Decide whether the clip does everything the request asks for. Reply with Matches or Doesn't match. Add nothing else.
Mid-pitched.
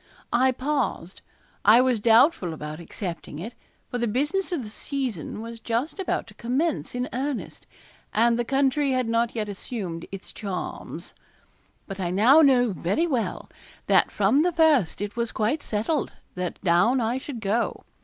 Doesn't match